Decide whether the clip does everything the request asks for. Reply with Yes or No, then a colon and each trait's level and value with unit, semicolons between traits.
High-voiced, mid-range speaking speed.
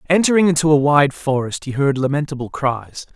No: medium, 145 Hz; average, 170 wpm